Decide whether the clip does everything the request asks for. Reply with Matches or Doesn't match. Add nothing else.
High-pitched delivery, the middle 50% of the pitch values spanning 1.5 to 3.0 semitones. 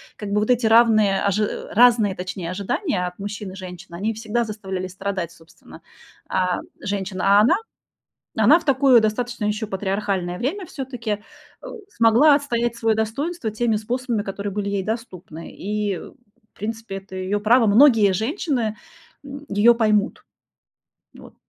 Doesn't match